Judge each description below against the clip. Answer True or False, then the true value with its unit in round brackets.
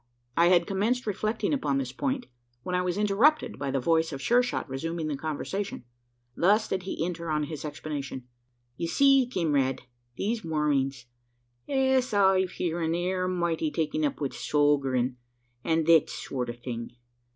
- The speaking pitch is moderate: True (165 Hz)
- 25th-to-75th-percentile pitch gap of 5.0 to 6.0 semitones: True (5.5 semitones)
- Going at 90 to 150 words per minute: False (160 wpm)